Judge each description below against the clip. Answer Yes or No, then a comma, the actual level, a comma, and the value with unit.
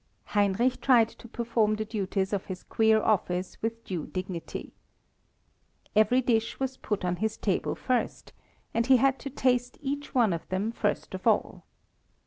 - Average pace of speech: Yes, average, 160 wpm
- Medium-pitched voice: No, high, 220 Hz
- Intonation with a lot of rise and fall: No, average, 4.1 semitones